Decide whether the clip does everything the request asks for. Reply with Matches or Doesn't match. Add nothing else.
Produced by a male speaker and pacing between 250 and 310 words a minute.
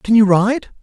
Doesn't match